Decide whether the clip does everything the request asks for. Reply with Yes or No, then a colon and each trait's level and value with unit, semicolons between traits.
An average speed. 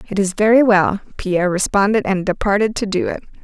Yes: average, 190 wpm